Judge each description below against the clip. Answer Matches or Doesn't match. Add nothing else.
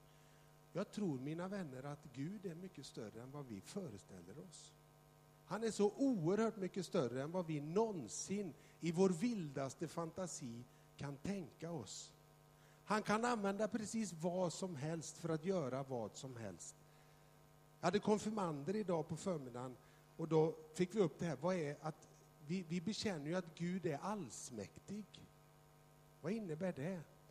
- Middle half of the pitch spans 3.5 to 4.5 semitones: Matches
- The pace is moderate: Matches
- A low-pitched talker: Doesn't match